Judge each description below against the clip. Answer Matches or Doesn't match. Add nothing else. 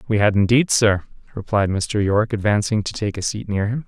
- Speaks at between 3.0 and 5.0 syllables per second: Doesn't match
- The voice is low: Matches